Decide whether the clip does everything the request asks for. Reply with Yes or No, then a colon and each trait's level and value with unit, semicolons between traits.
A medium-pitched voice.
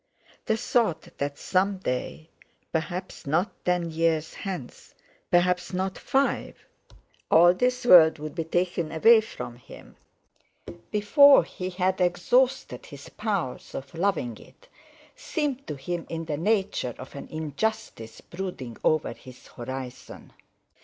Yes: medium, 175 Hz